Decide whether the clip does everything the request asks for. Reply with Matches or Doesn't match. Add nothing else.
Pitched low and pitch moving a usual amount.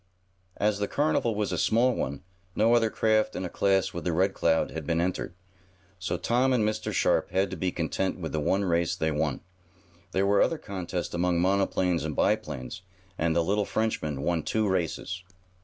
Matches